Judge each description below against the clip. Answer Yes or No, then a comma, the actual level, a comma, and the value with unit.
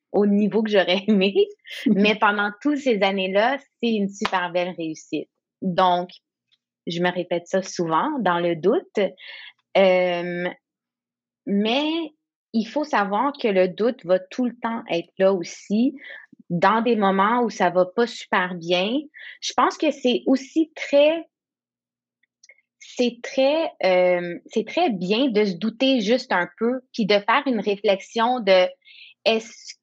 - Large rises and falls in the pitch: Yes, wide, 5.7 semitones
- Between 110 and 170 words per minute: Yes, average, 150 wpm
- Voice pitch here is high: Yes, high, 210 Hz